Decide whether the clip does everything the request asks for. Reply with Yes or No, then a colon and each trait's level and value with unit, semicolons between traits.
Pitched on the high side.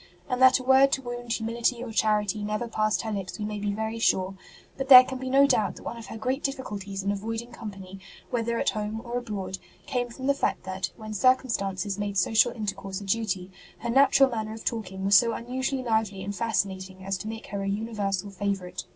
Yes: high, 220 Hz